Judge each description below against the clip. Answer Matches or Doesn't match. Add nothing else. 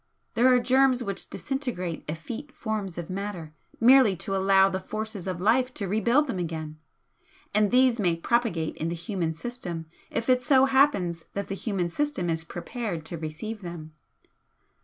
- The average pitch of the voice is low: Doesn't match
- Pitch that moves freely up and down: Matches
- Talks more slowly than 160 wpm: Doesn't match